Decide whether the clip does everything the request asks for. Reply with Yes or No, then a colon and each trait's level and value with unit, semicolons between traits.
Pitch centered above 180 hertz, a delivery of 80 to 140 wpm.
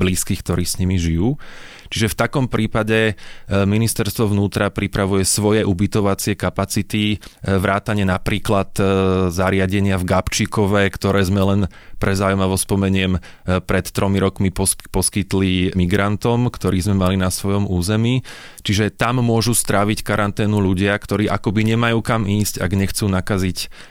No: low, 100 Hz; average, 125 wpm